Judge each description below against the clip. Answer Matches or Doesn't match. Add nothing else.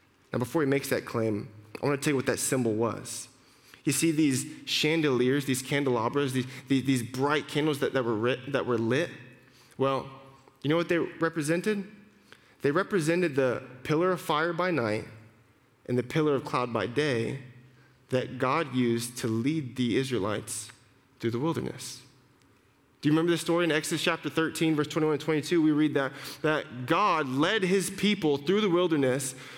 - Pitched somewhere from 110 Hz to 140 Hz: Matches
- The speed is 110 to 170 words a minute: Doesn't match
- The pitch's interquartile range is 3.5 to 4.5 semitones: Matches